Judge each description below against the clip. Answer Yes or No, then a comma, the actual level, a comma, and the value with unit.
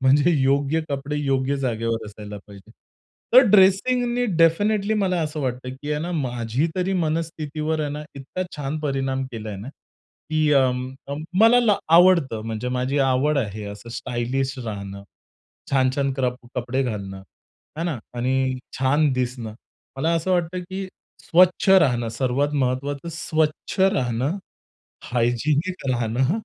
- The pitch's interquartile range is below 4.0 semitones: No, average, 4.8 semitones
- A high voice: No, low, 135 Hz